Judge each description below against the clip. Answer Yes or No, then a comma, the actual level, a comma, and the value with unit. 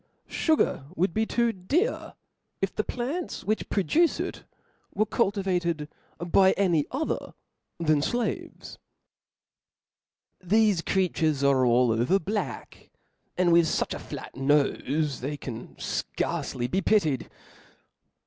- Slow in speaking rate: Yes, slow, 120 wpm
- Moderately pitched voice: Yes, medium, 180 Hz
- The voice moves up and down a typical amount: No, wide, 6.5 semitones